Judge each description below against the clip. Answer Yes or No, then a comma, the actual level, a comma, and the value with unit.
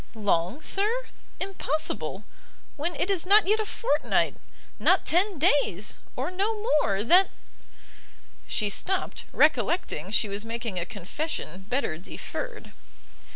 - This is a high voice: Yes, very high, 295 Hz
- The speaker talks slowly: Yes, slow, 125 wpm